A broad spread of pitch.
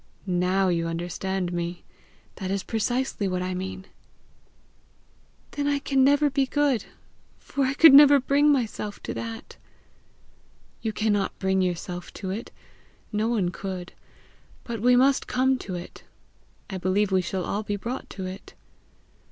Yes: wide, 6.0 semitones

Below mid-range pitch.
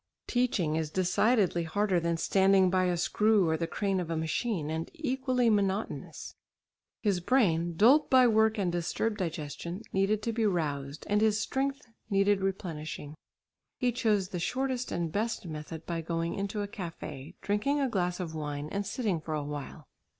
No: high, 190 Hz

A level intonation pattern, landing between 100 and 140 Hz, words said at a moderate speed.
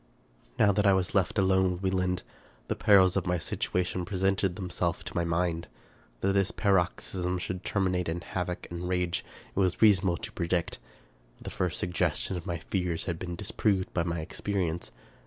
No: narrow, 1.7 semitones; very low, 90 Hz; average, 175 wpm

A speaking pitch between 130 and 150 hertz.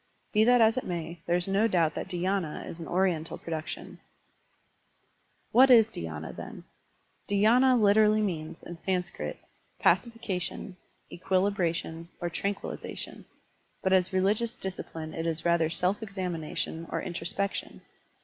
No: medium, 185 Hz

